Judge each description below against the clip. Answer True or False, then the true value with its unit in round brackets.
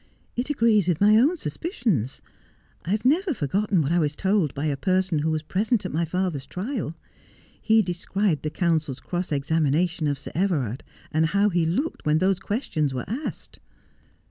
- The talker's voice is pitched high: False (175 Hz)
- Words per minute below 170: False (175 wpm)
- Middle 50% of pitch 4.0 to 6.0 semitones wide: True (5.4 semitones)